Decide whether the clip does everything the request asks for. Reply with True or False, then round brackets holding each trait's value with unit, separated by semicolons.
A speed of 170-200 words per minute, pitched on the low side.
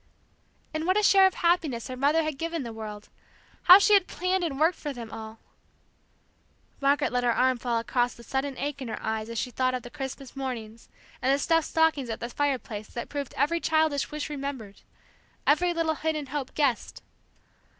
False (195 wpm; 275 Hz)